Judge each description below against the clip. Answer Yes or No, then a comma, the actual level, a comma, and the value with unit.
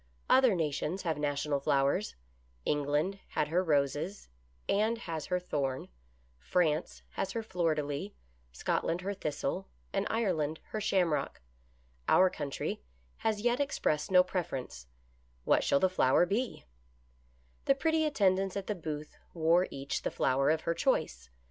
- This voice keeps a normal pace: Yes, average, 150 wpm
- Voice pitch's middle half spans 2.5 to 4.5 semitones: No, average, 5.3 semitones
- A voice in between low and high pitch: Yes, medium, 165 Hz